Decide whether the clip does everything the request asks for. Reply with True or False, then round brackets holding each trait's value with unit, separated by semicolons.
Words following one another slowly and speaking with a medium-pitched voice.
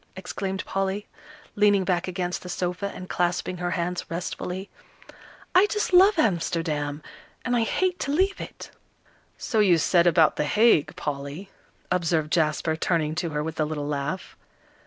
False (155 wpm; 180 Hz)